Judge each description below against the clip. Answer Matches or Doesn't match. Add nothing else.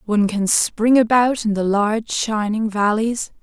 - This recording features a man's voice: Doesn't match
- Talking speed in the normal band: Matches